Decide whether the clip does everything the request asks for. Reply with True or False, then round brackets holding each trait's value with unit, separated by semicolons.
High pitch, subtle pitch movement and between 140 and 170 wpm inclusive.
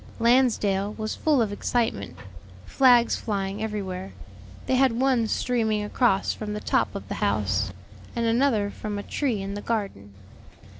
False (215 Hz; 3.4 semitones; 150 wpm)